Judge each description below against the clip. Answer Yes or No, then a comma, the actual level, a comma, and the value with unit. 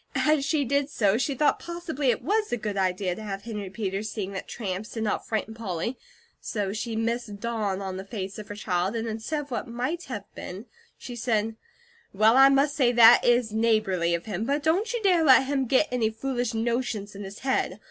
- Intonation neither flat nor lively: Yes, average, 4.5 semitones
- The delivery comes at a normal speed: No, fast, 215 wpm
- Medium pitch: No, high, 225 Hz